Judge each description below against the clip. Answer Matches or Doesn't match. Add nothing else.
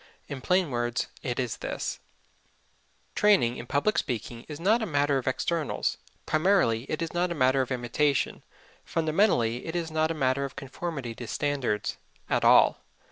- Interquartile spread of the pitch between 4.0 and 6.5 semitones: Matches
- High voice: Doesn't match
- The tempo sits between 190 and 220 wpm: Doesn't match